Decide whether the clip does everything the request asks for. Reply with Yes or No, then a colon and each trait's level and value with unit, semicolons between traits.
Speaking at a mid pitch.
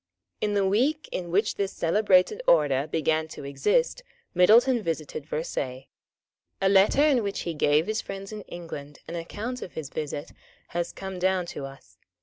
Yes: medium, 180 Hz